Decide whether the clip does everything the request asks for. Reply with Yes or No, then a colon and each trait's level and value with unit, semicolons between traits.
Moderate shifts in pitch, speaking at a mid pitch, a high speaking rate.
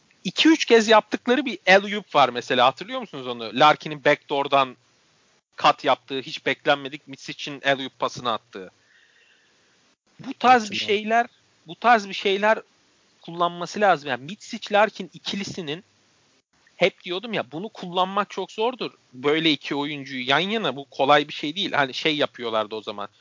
No: wide, 7.0 semitones; medium, 175 Hz; fast, 155 wpm